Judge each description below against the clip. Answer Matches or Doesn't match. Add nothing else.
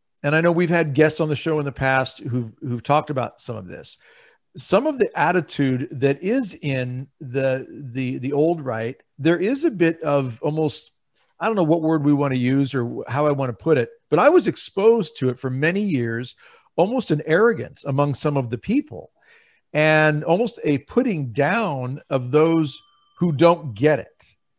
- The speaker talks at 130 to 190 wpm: Doesn't match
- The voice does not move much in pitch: Doesn't match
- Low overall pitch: Doesn't match